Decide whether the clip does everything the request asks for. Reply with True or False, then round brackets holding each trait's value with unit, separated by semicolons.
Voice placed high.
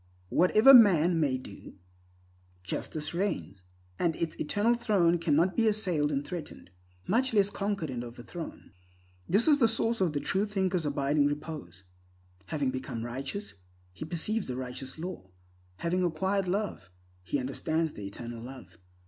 False (165 Hz)